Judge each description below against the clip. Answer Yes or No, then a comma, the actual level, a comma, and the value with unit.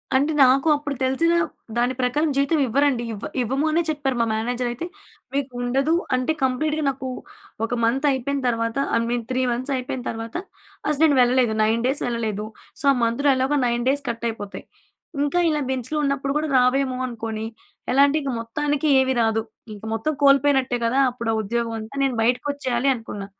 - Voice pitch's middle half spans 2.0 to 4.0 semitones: Yes, average, 3.1 semitones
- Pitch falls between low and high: No, very high, 255 Hz